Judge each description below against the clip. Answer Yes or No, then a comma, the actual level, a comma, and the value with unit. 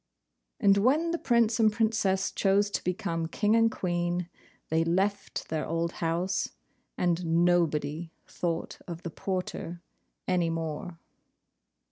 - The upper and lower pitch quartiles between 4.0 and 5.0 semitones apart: No, average, 3.5 semitones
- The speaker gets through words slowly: Yes, slow, 125 wpm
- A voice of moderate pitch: Yes, medium, 175 Hz